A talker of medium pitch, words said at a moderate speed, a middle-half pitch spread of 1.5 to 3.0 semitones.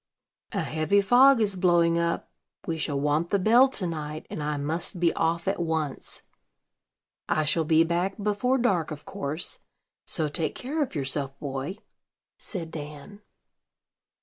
No: medium, 165 Hz; average, 150 wpm; average, 4.6 semitones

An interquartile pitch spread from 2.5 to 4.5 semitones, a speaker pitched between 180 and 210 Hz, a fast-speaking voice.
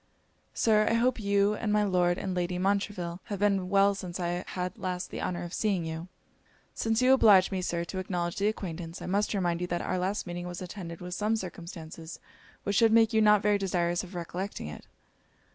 Yes: average, 2.9 semitones; medium, 185 Hz; fast, 210 wpm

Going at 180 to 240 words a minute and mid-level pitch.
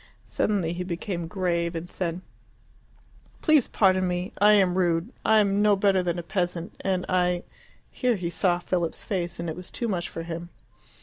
Yes: average, 185 wpm; medium, 180 Hz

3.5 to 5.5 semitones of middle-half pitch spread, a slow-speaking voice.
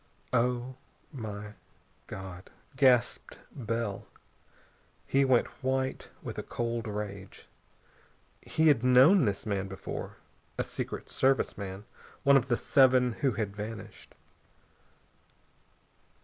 Yes: average, 4.1 semitones; slow, 105 wpm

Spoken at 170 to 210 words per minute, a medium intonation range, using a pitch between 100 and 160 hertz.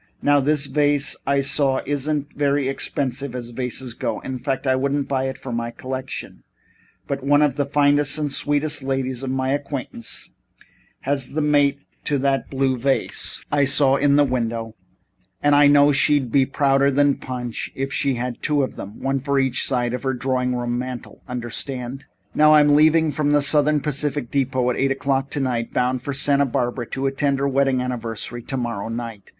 No: average, 185 wpm; narrow, 2.2 semitones; low, 135 Hz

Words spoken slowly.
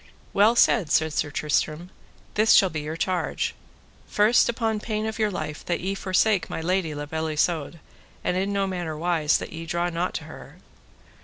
No: average, 185 wpm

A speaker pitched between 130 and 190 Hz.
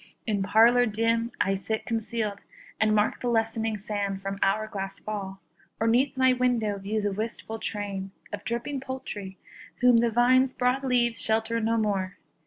No: high, 220 Hz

